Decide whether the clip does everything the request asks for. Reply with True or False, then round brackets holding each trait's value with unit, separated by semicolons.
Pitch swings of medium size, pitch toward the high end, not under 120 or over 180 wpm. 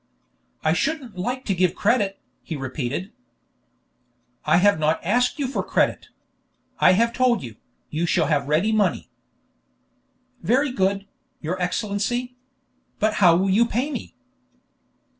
False (5.9 semitones; 195 Hz; 135 wpm)